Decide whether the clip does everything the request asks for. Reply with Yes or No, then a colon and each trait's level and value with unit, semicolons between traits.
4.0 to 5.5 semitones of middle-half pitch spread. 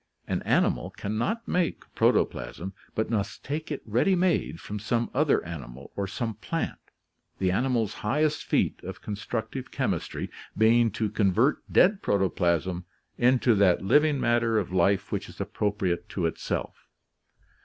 Yes: average, 5.1 semitones